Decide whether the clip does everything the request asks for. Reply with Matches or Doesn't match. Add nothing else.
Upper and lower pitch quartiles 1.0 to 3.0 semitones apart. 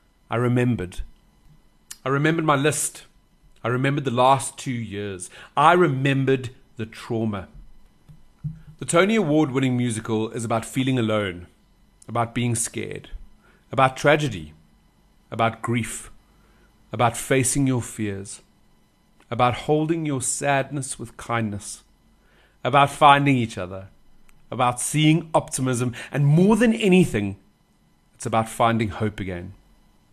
Doesn't match